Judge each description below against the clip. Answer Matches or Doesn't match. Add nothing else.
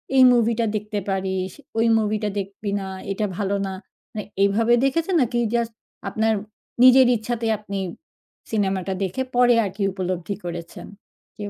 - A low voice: Doesn't match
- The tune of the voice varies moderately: Matches